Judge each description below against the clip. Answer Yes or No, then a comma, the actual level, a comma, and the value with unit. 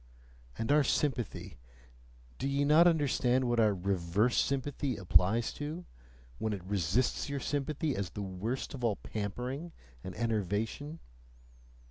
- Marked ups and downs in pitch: Yes, wide, 5.9 semitones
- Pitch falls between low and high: No, low, 120 Hz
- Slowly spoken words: Yes, slow, 130 wpm